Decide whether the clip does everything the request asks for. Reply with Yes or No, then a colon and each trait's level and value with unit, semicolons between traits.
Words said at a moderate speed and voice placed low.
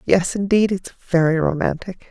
No: average, 145 wpm; medium, 180 Hz